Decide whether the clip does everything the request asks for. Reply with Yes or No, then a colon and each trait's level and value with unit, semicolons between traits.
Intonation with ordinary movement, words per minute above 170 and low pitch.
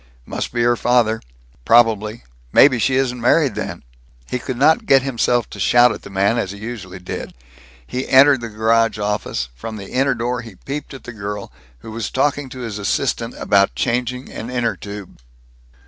Yes: average, 3.3 semitones; average, 185 wpm; low, 120 Hz